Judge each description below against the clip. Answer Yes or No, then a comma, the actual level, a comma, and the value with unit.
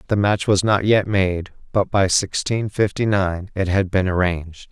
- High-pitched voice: No, very low, 95 Hz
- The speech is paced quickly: No, average, 190 wpm